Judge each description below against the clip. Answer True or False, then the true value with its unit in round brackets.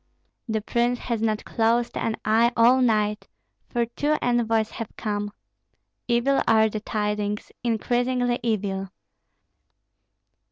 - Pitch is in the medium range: False (225 Hz)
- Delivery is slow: True (115 wpm)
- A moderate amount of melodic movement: False (2.1 semitones)